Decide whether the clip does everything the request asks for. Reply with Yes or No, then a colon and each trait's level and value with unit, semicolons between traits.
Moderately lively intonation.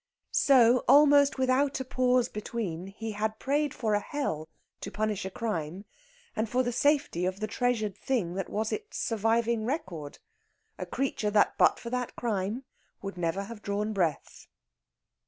Yes: average, 4.3 semitones